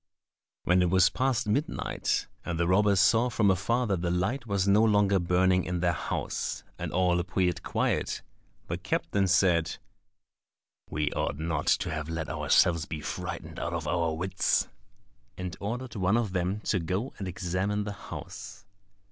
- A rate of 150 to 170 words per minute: Yes, average, 165 wpm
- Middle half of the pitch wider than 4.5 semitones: No, average, 2.9 semitones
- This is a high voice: No, very low, 95 Hz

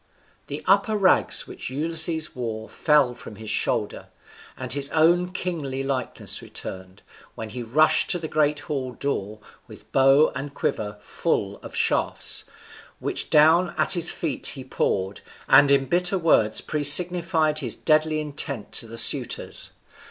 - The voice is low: No, medium, 145 Hz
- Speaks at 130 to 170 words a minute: Yes, average, 145 wpm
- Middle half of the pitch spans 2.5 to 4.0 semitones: No, average, 4.4 semitones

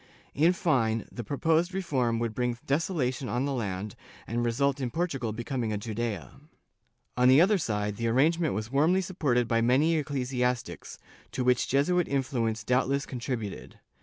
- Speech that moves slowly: No, average, 155 wpm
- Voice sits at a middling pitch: No, low, 125 Hz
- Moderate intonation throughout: Yes, average, 3.9 semitones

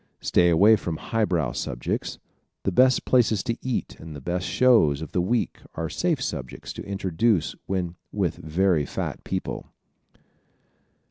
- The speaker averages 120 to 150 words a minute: Yes, average, 145 wpm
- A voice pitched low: Yes, very low, 90 Hz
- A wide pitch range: Yes, wide, 5.8 semitones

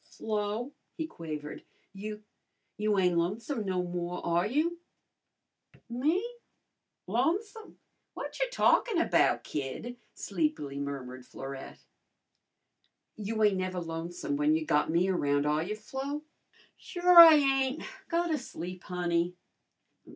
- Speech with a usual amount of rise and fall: No, wide, 8.7 semitones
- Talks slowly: Yes, slow, 115 wpm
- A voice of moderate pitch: No, high, 195 Hz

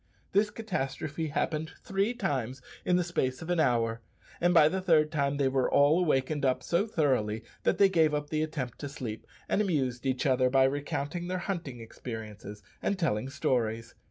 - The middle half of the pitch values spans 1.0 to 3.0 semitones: No, average, 4.9 semitones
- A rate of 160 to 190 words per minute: Yes, average, 185 wpm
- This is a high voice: No, medium, 145 Hz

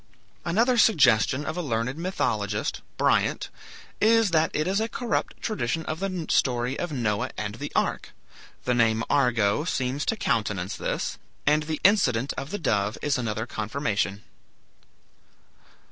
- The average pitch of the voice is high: No, low, 135 Hz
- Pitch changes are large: Yes, wide, 7.3 semitones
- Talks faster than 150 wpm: No, average, 145 wpm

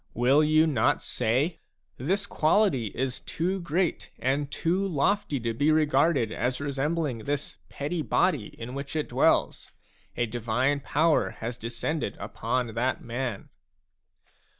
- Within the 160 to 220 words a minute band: No, slow, 135 wpm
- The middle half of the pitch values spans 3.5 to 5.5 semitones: Yes, average, 4.7 semitones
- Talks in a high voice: No, medium, 140 Hz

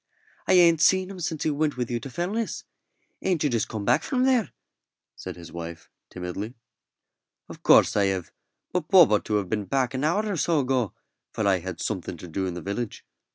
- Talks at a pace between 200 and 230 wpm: Yes, fast, 205 wpm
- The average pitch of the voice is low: Yes, low, 125 Hz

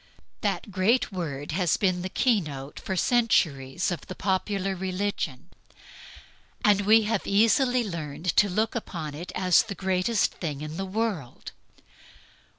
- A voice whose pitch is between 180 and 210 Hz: Yes, medium, 185 Hz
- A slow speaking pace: No, average, 145 wpm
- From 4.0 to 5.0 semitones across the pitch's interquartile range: Yes, average, 4.3 semitones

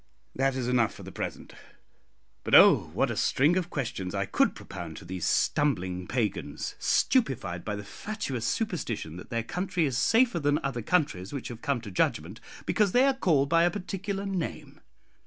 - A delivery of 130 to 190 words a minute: Yes, average, 180 wpm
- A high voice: No, low, 135 Hz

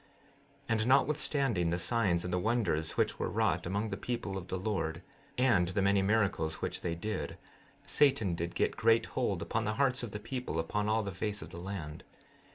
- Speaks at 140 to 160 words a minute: No, average, 200 wpm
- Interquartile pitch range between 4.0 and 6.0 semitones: Yes, average, 4.5 semitones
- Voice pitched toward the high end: No, low, 100 Hz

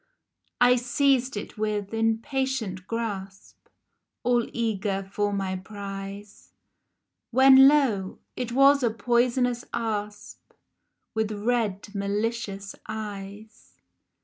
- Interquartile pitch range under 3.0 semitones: No, average, 3.4 semitones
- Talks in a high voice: Yes, high, 220 Hz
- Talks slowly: Yes, slow, 95 wpm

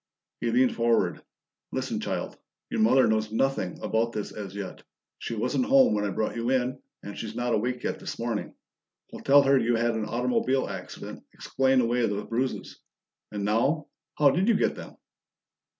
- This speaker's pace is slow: No, average, 180 wpm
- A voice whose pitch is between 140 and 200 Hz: No, low, 120 Hz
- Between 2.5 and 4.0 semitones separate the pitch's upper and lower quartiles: Yes, average, 3.2 semitones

